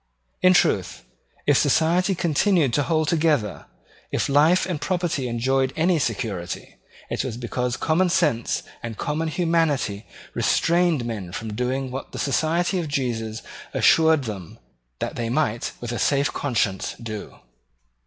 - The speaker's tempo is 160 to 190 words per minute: No, average, 140 wpm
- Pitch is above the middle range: No, medium, 140 Hz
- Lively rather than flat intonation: Yes, wide, 5.8 semitones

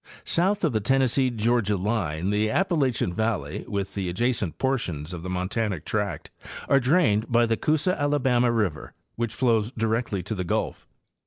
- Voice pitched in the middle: No, low, 115 Hz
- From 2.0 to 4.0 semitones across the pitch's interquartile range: No, average, 4.7 semitones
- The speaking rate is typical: Yes, average, 160 wpm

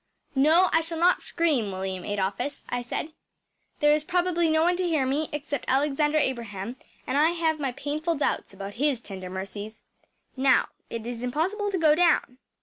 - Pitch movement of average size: No, wide, 5.7 semitones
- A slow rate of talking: No, average, 175 wpm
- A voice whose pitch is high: Yes, very high, 285 Hz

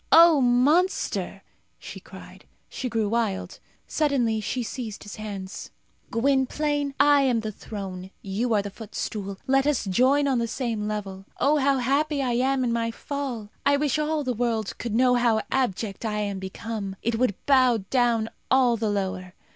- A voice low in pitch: No, high, 235 Hz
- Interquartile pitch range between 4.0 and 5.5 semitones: Yes, average, 4.4 semitones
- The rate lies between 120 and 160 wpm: No, average, 170 wpm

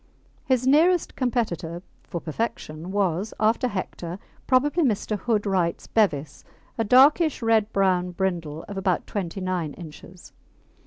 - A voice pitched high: Yes, high, 195 Hz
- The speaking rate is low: Yes, slow, 120 wpm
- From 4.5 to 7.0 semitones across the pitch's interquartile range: Yes, average, 5.1 semitones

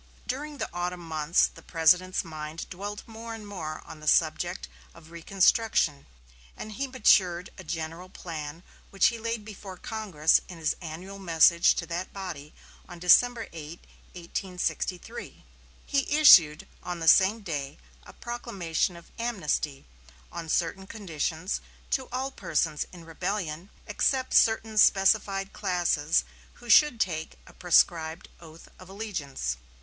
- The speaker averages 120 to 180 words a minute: Yes, slow, 135 wpm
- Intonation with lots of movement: No, average, 4.5 semitones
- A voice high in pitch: No, medium, 180 Hz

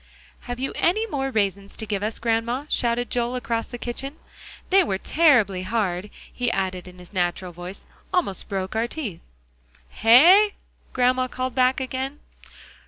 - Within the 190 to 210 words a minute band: No, average, 155 wpm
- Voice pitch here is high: Yes, high, 235 Hz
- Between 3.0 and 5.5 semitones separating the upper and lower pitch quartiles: Yes, average, 5.0 semitones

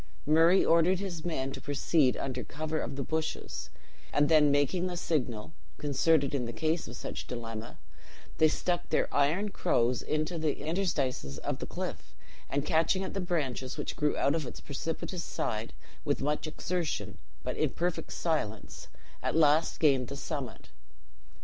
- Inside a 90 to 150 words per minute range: No, average, 160 wpm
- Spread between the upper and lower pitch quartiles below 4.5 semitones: Yes, average, 3.5 semitones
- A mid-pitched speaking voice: Yes, medium, 150 Hz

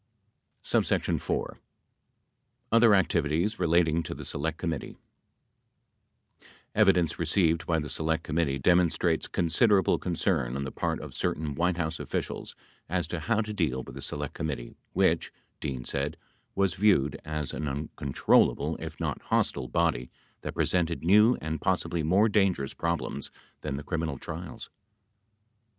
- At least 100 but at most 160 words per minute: Yes, average, 140 wpm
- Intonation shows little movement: No, average, 3.6 semitones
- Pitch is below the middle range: Yes, very low, 80 Hz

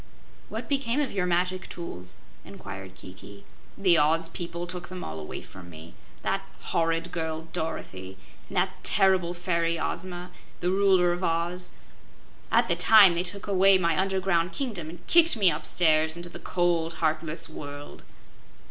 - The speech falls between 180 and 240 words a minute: No, average, 155 wpm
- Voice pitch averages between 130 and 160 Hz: No, medium, 175 Hz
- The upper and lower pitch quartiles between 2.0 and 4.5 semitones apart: Yes, narrow, 2.6 semitones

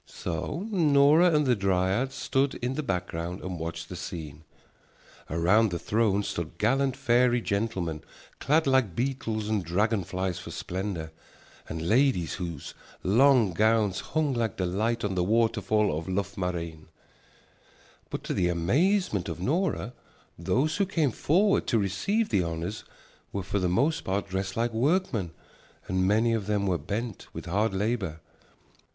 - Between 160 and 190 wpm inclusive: No, average, 150 wpm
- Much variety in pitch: Yes, wide, 6.1 semitones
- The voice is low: Yes, low, 105 Hz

